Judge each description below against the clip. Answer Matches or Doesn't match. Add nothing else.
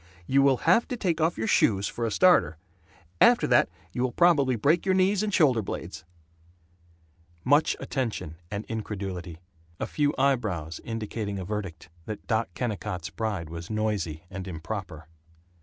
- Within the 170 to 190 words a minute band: Doesn't match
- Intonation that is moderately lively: Doesn't match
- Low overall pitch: Matches